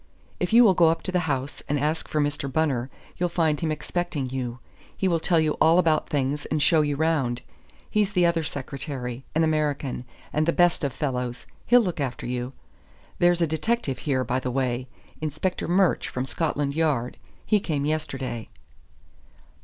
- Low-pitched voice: No, medium, 150 Hz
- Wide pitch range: No, average, 4.1 semitones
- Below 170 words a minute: No, average, 180 wpm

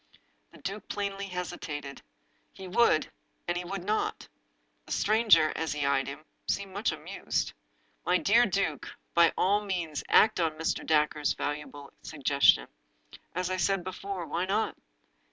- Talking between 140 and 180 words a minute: Yes, average, 155 wpm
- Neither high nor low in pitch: Yes, medium, 180 Hz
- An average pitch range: Yes, average, 4.4 semitones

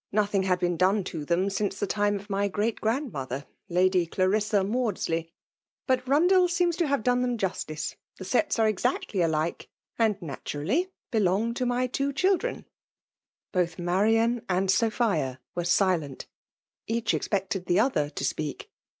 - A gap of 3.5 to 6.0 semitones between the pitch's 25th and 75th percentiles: Yes, average, 5.0 semitones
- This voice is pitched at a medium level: No, high, 200 Hz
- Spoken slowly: No, average, 160 wpm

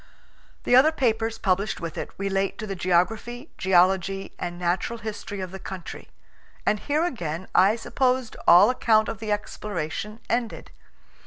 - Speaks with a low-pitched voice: No, high, 205 Hz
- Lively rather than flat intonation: No, average, 3.7 semitones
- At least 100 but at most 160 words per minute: Yes, average, 150 wpm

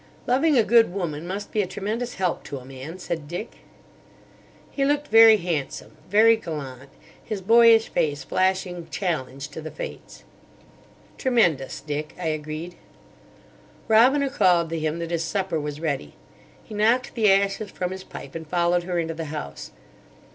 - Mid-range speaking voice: Yes, medium, 175 Hz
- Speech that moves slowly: No, average, 160 wpm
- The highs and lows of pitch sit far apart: Yes, wide, 5.7 semitones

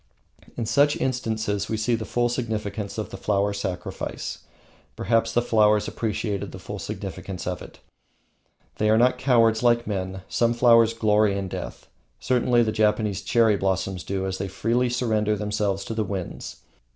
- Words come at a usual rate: Yes, average, 165 wpm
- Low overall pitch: Yes, low, 110 Hz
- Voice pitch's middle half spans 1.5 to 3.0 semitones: Yes, average, 2.7 semitones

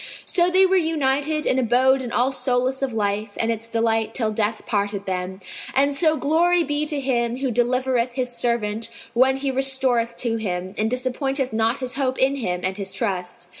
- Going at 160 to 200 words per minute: Yes, average, 190 wpm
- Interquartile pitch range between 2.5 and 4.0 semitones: Yes, average, 3.4 semitones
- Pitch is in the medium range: No, very high, 250 Hz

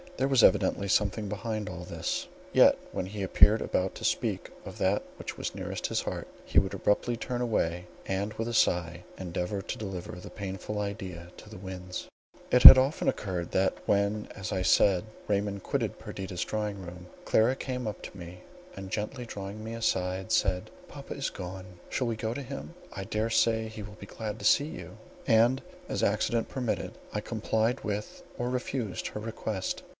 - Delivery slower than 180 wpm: No, average, 185 wpm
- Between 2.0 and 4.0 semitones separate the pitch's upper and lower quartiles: Yes, average, 3.0 semitones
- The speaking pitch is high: No, low, 105 Hz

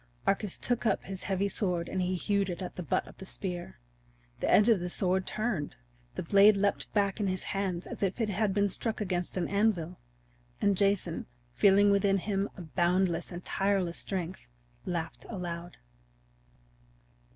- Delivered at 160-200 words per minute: Yes, average, 170 wpm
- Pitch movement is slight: Yes, narrow, 2.2 semitones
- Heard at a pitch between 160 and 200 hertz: Yes, high, 190 Hz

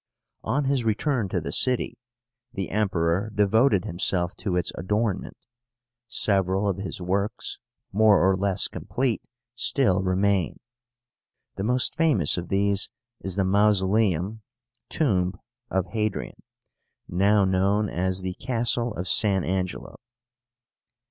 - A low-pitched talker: Yes, low, 100 Hz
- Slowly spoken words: Yes, slow, 120 wpm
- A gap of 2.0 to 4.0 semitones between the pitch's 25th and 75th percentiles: Yes, average, 2.8 semitones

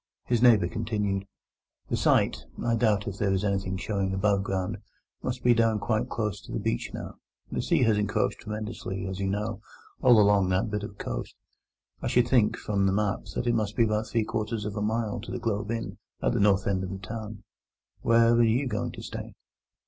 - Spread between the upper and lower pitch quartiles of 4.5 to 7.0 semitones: No, narrow, 2.5 semitones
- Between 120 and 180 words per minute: No, fast, 205 wpm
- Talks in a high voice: No, low, 105 Hz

